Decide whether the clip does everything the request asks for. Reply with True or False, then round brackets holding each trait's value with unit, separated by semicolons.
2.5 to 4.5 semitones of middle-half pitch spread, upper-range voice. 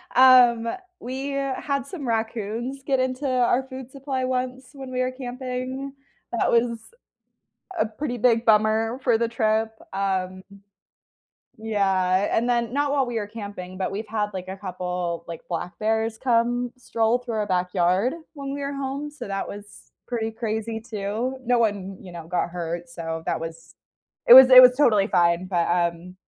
False (4.9 semitones; 225 Hz)